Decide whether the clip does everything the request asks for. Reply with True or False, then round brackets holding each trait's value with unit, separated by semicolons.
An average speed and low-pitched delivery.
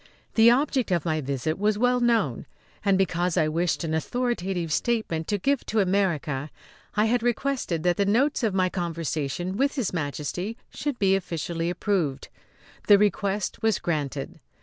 False (160 wpm; 190 Hz)